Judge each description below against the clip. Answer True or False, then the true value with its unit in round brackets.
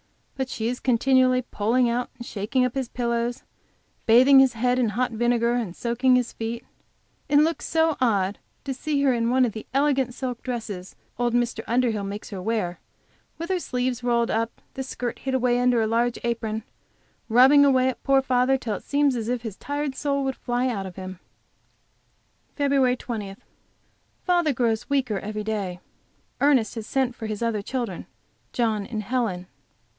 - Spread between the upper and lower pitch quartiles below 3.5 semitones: True (2.8 semitones)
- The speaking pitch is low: False (245 Hz)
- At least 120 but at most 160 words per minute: False (180 wpm)